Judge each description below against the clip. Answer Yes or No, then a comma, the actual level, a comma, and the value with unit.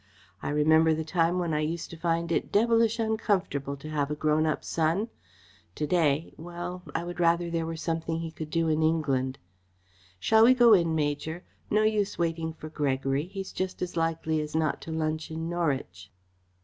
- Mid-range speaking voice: Yes, medium, 165 Hz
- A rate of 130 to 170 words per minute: No, average, 190 wpm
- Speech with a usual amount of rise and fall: No, narrow, 2.3 semitones